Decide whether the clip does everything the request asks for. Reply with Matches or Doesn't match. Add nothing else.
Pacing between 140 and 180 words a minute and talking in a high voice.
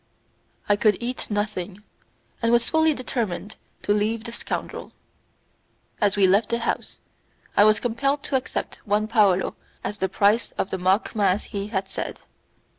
Matches